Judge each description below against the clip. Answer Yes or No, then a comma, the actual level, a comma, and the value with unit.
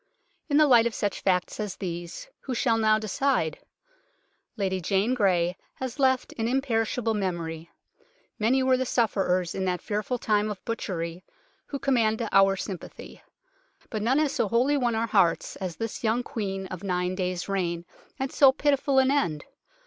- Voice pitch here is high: Yes, high, 215 Hz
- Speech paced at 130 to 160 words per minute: No, average, 170 wpm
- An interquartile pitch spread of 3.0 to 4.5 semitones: No, average, 5.2 semitones